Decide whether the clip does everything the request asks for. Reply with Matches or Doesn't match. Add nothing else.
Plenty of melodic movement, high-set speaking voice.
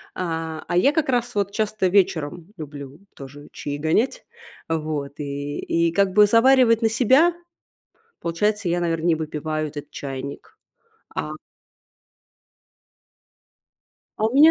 Doesn't match